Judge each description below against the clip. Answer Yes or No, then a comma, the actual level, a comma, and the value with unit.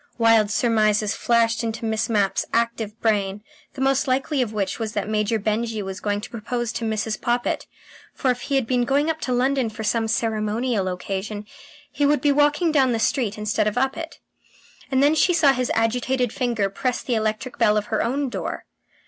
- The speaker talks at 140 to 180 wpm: No, average, 200 wpm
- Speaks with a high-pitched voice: Yes, high, 230 Hz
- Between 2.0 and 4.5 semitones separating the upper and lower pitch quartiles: Yes, average, 3.4 semitones